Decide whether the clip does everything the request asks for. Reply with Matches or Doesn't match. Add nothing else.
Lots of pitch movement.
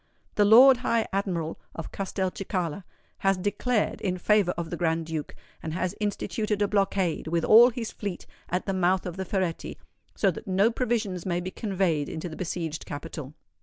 Doesn't match